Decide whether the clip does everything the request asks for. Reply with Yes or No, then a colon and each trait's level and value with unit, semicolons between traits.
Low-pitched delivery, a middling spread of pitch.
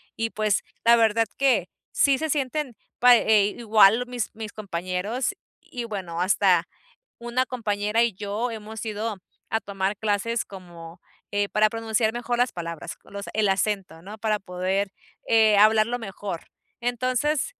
No: high, 215 Hz; average, 3.0 semitones